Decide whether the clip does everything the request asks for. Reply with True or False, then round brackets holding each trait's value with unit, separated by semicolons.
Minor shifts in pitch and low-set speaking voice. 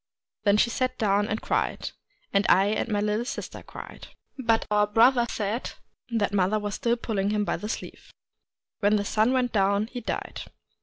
False (2.3 semitones; 210 Hz)